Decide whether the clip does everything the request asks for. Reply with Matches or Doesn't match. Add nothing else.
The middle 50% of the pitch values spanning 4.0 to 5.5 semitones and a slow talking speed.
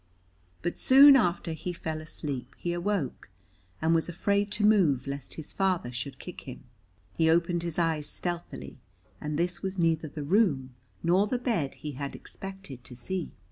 Doesn't match